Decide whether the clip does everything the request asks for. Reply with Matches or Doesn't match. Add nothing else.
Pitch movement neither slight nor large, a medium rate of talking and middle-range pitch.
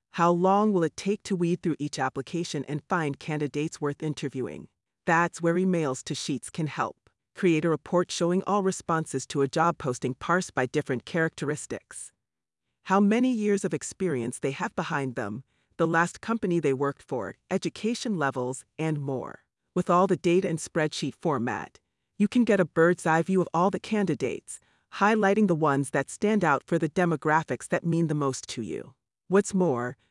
Matches